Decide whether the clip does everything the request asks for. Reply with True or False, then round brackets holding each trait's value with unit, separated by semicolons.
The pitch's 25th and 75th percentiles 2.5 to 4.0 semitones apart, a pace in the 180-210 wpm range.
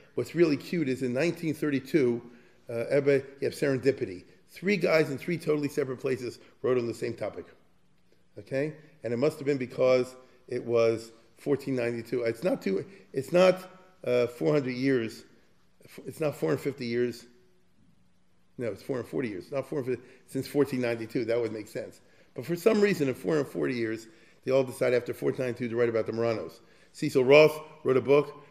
False (3.7 semitones; 165 wpm)